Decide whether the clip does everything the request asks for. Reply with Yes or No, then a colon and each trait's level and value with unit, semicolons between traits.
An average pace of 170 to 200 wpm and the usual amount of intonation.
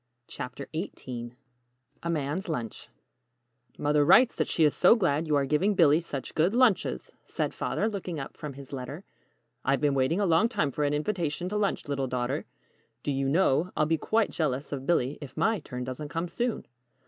Yes: average, 195 wpm; average, 4.7 semitones